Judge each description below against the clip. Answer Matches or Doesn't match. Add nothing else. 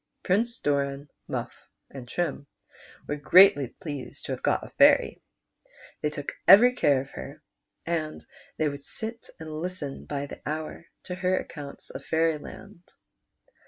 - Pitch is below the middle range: Doesn't match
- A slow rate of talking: Doesn't match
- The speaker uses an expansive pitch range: Doesn't match